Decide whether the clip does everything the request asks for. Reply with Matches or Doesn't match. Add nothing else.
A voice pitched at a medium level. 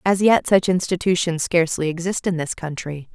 Matches